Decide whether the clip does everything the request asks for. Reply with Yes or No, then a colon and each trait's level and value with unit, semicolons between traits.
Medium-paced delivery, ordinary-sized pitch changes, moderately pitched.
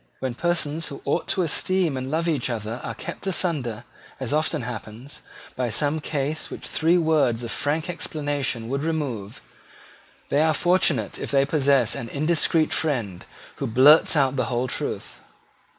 Yes: average, 160 wpm; average, 4.3 semitones; medium, 145 Hz